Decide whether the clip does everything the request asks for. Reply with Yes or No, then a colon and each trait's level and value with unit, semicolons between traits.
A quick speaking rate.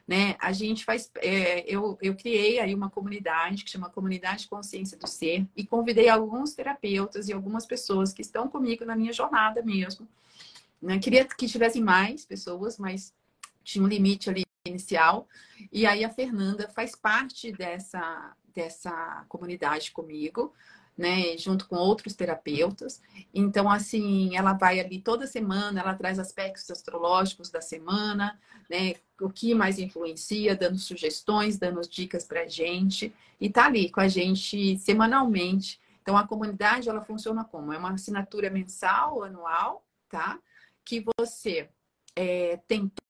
No: average, 150 wpm